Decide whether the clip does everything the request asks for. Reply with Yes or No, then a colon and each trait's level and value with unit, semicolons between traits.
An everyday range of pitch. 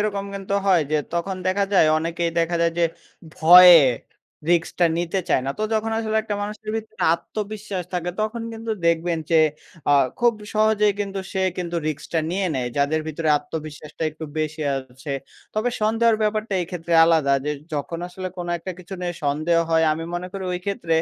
Yes: average, 4.1 semitones